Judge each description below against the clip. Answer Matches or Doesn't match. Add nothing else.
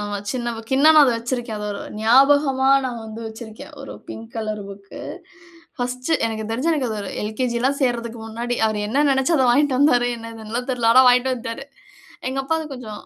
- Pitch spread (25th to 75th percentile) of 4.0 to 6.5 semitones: Doesn't match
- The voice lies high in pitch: Matches